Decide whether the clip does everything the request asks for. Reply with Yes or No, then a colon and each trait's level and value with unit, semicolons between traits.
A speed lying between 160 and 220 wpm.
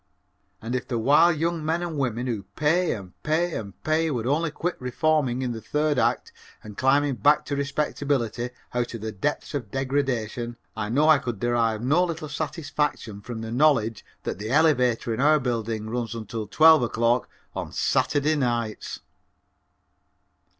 Yes: average, 170 wpm